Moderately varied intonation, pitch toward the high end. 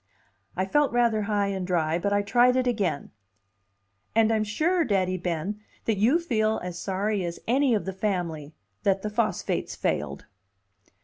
Yes: average, 3.7 semitones; high, 205 Hz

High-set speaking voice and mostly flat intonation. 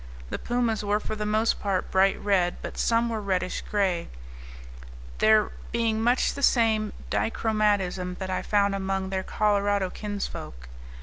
Yes: high, 205 Hz; narrow, 2.3 semitones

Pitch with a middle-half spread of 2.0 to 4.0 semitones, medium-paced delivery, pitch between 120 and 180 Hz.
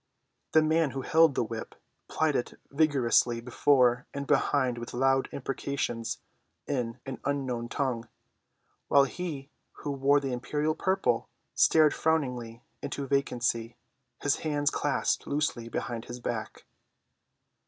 No: average, 3.2 semitones; slow, 125 wpm; low, 135 Hz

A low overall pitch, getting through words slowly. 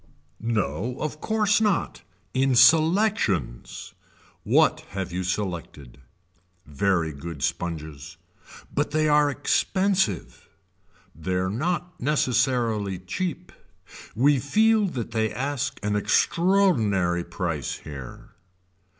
Yes: low, 115 Hz; slow, 100 wpm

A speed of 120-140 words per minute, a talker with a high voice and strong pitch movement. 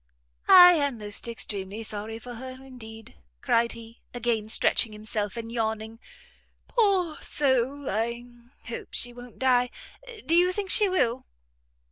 No: slow, 135 wpm; high, 235 Hz; average, 3.3 semitones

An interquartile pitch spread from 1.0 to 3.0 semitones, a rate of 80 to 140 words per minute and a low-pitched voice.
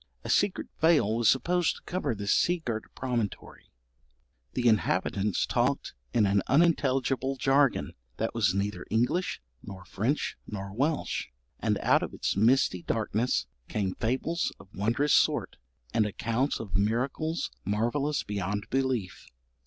No: average, 5.0 semitones; slow, 135 wpm; low, 115 Hz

